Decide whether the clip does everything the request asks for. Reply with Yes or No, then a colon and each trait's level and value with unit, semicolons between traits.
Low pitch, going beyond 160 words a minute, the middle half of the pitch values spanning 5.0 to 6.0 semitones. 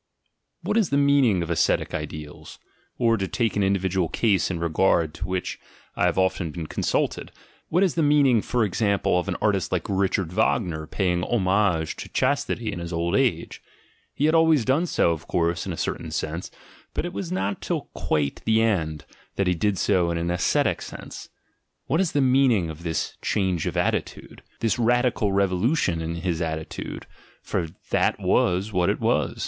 Yes: very low, 95 Hz; average, 190 wpm; wide, 5.4 semitones